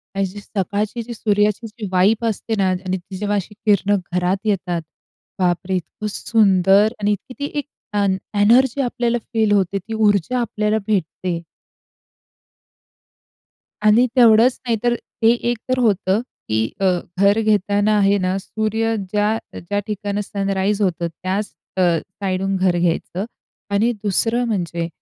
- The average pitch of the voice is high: Yes, high, 205 Hz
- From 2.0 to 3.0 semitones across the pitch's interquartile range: Yes, average, 2.7 semitones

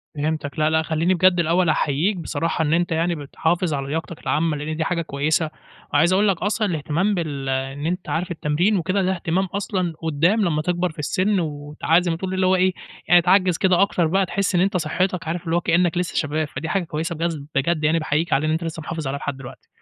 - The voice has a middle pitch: Yes, medium, 165 Hz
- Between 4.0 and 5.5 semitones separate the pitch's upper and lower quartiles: No, average, 2.8 semitones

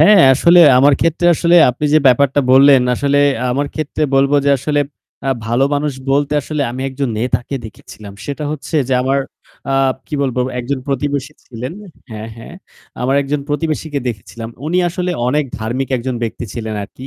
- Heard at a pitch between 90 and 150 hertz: Yes, medium, 140 Hz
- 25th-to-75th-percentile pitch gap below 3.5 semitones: Yes, average, 3.0 semitones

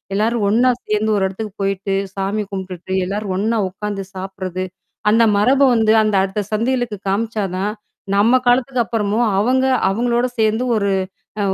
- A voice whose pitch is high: Yes, high, 210 Hz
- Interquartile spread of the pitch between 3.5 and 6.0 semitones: No, average, 2.9 semitones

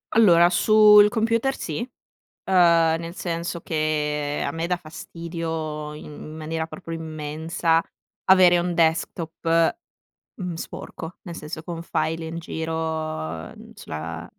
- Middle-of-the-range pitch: Yes, medium, 165 Hz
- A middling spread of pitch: No, narrow, 1.7 semitones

